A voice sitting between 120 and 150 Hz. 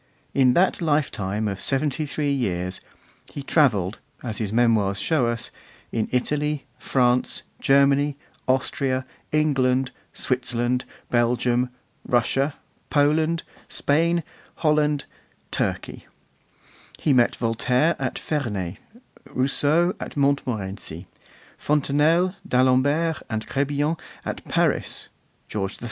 Yes: low, 135 Hz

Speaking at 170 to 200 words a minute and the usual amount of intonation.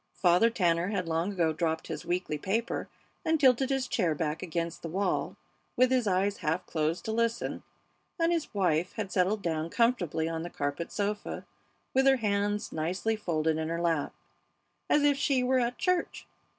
No: average, 175 wpm; wide, 6.0 semitones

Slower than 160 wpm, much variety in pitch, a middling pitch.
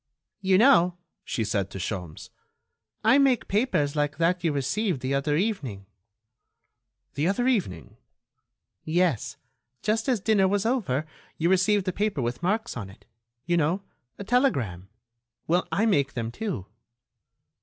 Yes: average, 145 wpm; wide, 7.6 semitones; medium, 175 Hz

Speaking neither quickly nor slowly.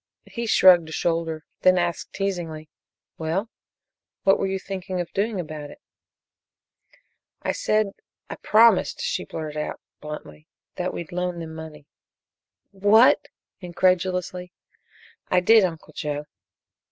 No: slow, 130 wpm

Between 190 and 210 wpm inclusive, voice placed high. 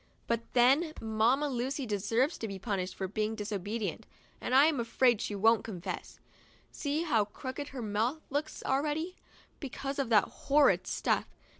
No: average, 150 wpm; high, 240 Hz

